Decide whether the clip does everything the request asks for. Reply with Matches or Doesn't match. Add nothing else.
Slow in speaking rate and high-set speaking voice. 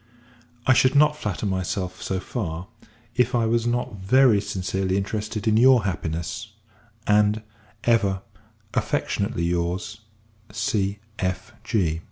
Doesn't match